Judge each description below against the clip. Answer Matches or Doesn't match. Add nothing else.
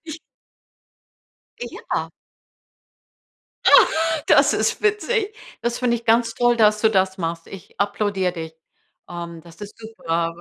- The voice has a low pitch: Doesn't match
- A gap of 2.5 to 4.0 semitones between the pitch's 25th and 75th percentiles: Doesn't match